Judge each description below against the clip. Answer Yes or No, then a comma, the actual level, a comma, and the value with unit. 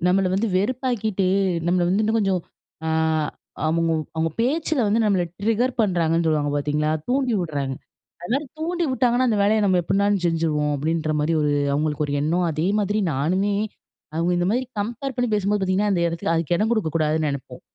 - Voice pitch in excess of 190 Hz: No, medium, 185 Hz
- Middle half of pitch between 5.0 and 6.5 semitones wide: Yes, wide, 5.4 semitones